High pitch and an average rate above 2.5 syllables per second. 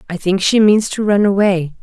Yes: high, 195 Hz; 5.1 syllables/s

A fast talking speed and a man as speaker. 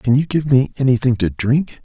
Yes: fast, 230 wpm; male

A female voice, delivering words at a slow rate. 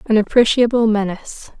Yes: female; slow, 115 wpm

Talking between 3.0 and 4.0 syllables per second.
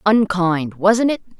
Yes: 3.5 syllables/s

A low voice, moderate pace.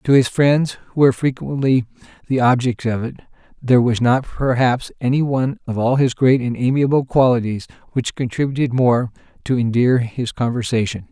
Yes: low, 125 Hz; average, 160 wpm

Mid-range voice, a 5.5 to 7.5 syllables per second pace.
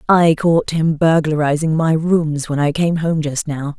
No: medium, 155 Hz; 4.1 syllables/s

